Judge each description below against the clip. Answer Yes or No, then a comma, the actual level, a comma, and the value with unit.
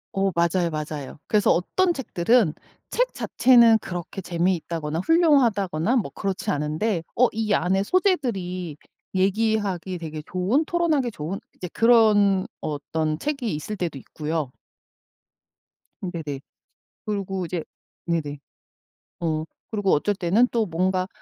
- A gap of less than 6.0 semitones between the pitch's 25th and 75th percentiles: Yes, average, 5.3 semitones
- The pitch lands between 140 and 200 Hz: Yes, high, 190 Hz